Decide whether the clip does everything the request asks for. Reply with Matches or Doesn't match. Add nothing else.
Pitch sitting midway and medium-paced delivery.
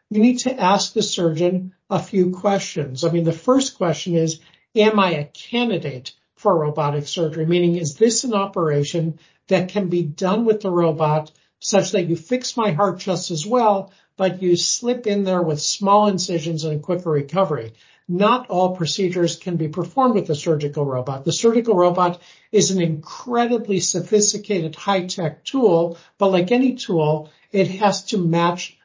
Matches